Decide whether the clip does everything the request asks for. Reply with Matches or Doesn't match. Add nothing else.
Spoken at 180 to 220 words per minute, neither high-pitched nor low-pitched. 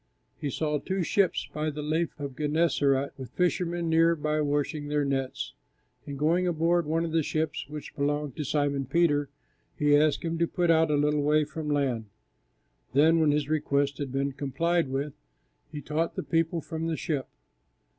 Matches